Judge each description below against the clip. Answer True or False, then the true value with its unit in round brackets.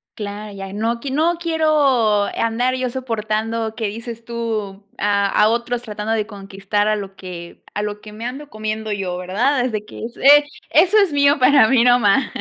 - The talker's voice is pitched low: False (225 Hz)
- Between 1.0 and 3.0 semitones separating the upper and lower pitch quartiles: False (3.6 semitones)